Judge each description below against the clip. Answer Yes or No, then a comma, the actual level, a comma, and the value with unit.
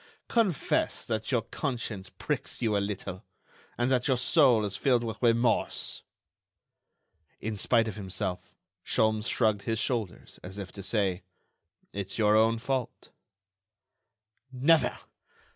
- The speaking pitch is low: Yes, low, 110 Hz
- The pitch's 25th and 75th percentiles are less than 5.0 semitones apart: Yes, average, 3.4 semitones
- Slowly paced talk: Yes, slow, 125 wpm